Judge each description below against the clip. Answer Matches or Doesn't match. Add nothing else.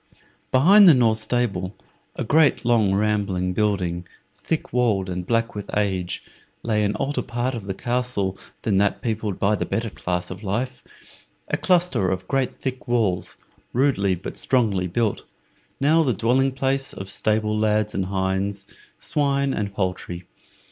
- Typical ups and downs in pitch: Matches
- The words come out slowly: Doesn't match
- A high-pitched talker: Doesn't match